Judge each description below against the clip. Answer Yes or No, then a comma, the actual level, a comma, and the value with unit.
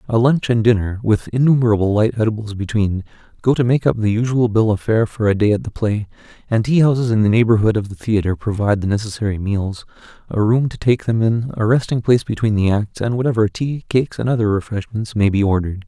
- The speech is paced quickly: Yes, fast, 225 wpm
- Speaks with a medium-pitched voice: No, low, 110 Hz